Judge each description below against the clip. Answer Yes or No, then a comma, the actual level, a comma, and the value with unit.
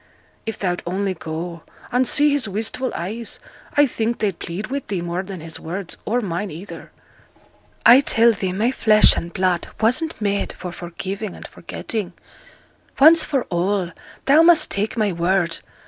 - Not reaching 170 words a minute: Yes, average, 160 wpm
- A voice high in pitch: Yes, high, 200 Hz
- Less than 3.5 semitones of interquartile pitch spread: No, average, 4.9 semitones